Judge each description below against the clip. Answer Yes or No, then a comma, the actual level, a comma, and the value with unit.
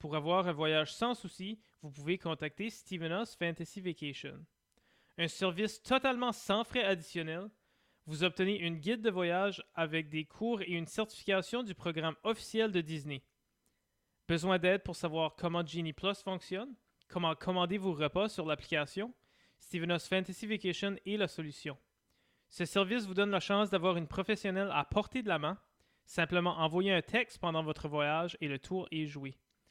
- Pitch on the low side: No, medium, 180 Hz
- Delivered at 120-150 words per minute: No, average, 165 wpm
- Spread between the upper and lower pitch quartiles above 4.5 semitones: No, average, 3.8 semitones